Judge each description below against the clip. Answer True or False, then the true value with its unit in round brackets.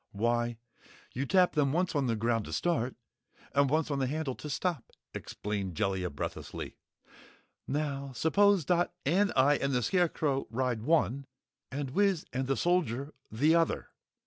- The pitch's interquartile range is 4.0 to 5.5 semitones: True (5.2 semitones)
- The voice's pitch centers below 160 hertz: True (140 Hz)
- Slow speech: False (155 wpm)